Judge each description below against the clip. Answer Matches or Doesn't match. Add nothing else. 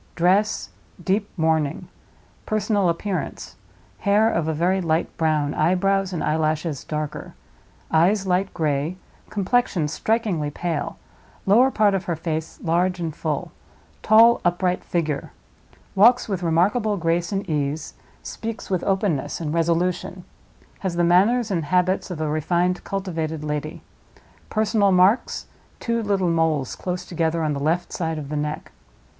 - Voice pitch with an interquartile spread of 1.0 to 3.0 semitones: Doesn't match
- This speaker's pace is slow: Matches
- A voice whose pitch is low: Doesn't match